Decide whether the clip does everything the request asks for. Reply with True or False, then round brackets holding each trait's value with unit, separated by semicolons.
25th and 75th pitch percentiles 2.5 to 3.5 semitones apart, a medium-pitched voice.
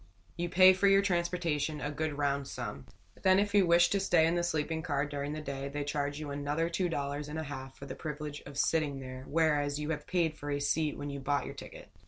True (2.9 semitones; 150 Hz)